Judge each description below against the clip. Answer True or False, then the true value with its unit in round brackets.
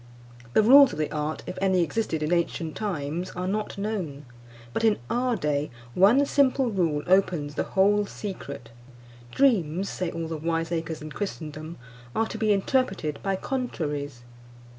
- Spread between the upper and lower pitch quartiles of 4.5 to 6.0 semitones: True (5.4 semitones)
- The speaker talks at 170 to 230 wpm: False (155 wpm)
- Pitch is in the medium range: True (180 Hz)